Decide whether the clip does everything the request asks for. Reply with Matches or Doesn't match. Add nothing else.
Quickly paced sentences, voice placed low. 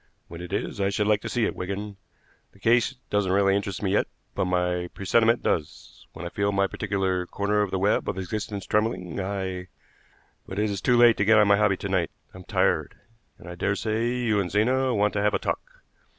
Matches